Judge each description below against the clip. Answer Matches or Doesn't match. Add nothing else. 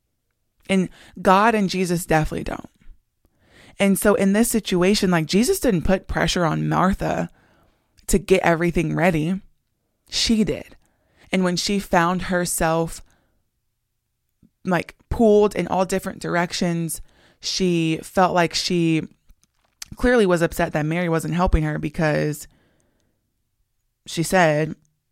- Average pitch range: Matches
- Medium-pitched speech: Matches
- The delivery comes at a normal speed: Doesn't match